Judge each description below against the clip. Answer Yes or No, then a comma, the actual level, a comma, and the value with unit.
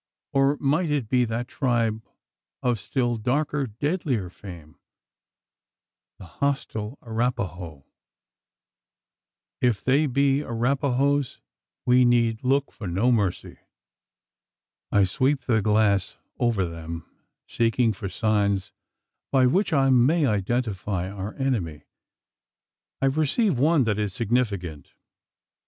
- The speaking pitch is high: No, low, 120 Hz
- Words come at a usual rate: No, slow, 110 wpm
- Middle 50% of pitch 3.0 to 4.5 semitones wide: No, average, 5.1 semitones